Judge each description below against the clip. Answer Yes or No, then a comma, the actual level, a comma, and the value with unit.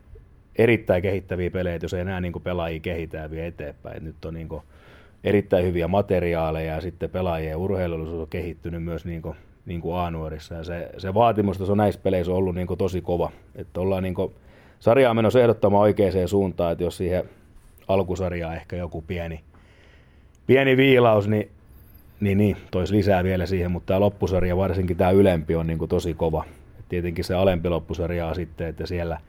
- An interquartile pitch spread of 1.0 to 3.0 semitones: Yes, average, 2.7 semitones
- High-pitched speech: No, very low, 90 Hz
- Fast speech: Yes, fast, 170 wpm